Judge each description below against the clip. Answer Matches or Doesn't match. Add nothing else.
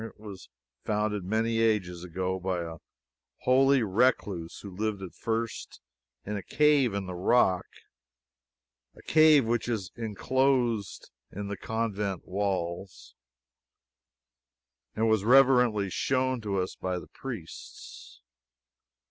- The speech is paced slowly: Matches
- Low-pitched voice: Matches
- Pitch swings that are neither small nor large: Matches